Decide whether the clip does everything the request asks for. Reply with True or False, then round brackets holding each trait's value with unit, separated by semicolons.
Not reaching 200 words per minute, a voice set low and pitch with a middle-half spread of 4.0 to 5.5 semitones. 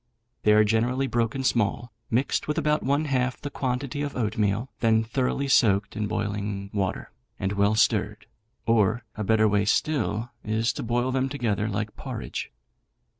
False (160 wpm; 115 Hz; 3.6 semitones)